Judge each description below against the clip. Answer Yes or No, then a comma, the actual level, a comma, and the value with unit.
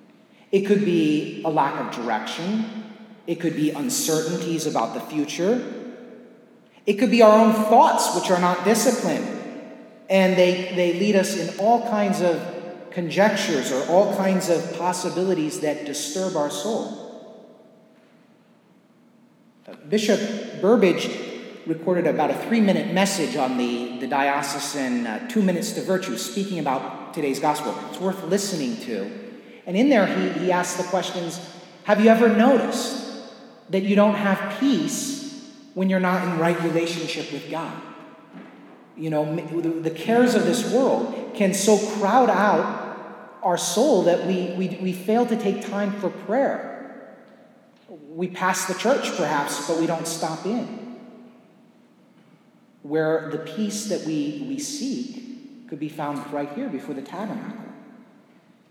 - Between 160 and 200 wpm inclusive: No, average, 145 wpm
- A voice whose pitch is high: Yes, high, 195 Hz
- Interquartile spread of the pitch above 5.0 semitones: Yes, wide, 5.5 semitones